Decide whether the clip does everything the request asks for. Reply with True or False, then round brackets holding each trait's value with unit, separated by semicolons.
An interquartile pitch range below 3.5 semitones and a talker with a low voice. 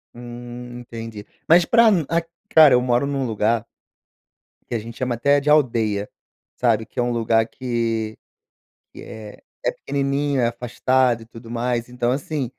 True (2.8 semitones; 120 Hz)